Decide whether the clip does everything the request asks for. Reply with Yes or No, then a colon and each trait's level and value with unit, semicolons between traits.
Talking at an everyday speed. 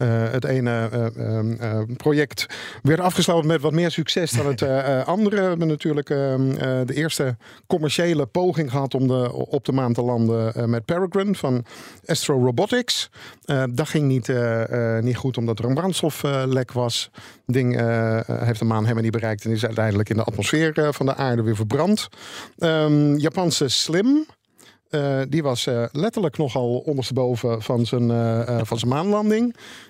Yes: average, 185 wpm